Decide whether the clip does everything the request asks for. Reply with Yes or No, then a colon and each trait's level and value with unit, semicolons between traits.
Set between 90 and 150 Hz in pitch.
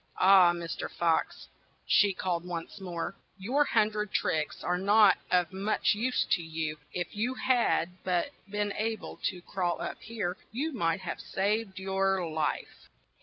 No: high, 190 Hz